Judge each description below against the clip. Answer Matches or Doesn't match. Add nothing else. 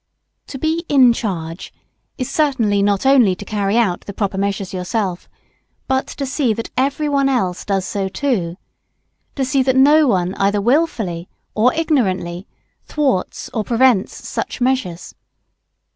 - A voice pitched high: Matches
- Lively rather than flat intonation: Matches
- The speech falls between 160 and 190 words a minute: Doesn't match